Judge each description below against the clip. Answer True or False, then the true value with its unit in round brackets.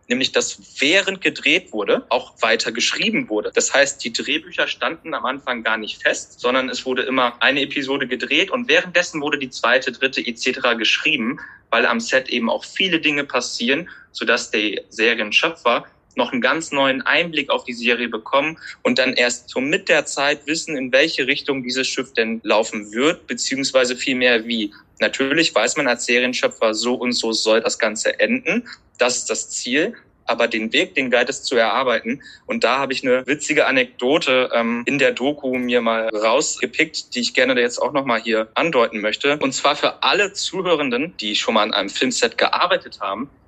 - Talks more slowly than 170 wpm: False (185 wpm)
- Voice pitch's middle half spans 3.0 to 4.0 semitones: True (3.3 semitones)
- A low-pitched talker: True (130 Hz)